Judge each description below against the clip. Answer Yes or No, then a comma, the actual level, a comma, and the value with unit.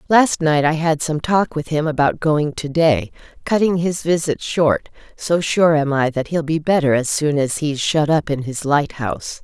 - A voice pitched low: No, medium, 155 Hz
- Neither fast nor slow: No, fast, 210 wpm